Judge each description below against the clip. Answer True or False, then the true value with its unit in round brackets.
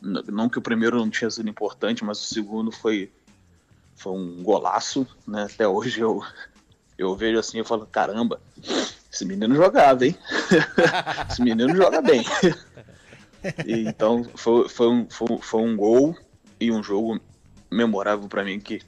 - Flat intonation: True (1.8 semitones)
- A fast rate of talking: False (155 wpm)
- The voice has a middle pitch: False (110 Hz)